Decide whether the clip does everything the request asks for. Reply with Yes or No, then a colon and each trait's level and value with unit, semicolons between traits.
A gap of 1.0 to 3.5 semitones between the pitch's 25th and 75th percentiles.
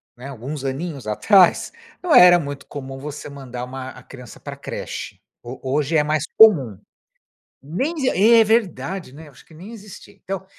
No: wide, 5.4 semitones